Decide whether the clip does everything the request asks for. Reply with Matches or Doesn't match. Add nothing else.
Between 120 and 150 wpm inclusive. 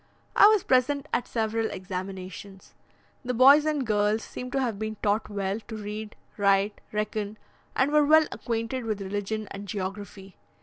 Doesn't match